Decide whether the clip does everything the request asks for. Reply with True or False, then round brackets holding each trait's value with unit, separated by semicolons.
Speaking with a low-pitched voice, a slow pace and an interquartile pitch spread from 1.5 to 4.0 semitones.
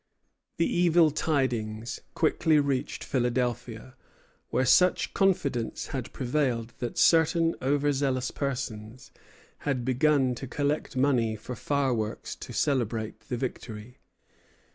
True (130 Hz; 110 wpm; 3.5 semitones)